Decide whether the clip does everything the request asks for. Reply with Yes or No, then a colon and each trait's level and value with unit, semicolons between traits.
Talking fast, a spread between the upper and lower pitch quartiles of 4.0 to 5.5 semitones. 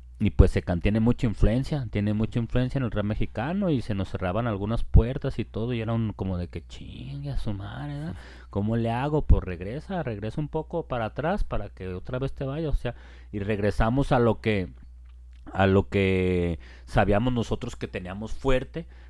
Yes: fast, 195 wpm; average, 5.0 semitones